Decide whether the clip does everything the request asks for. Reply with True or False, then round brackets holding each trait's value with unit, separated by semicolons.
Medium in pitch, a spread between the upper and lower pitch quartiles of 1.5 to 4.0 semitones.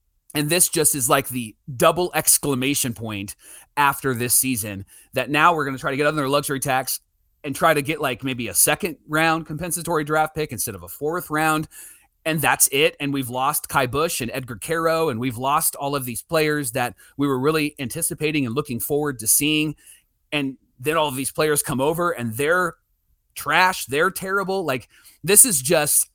True (145 Hz; 3.4 semitones)